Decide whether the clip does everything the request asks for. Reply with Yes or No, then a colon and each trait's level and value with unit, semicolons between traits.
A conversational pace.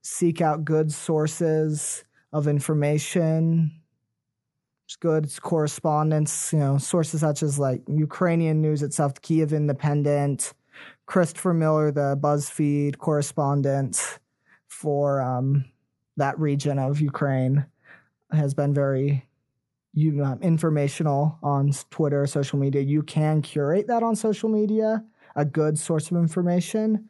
No: slow, 115 wpm